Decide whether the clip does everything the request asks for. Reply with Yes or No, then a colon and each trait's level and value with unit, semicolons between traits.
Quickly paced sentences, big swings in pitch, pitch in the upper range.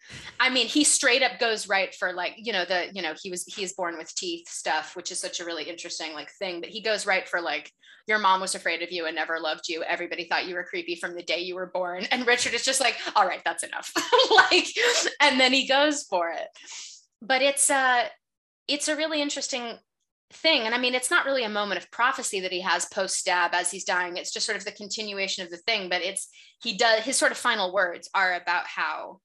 Yes: fast, 245 wpm; wide, 6.7 semitones; high, 205 Hz